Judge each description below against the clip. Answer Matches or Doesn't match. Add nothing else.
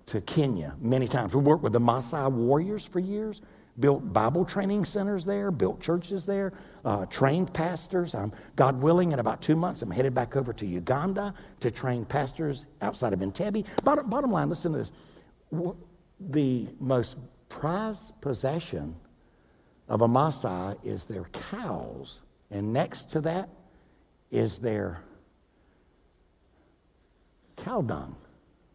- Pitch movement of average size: Doesn't match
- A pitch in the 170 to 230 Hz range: Doesn't match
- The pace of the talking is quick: Doesn't match